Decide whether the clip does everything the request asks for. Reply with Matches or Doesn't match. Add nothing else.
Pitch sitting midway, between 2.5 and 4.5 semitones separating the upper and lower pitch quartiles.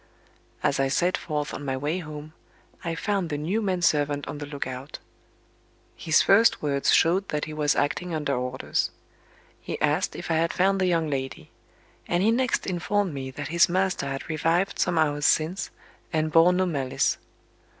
Matches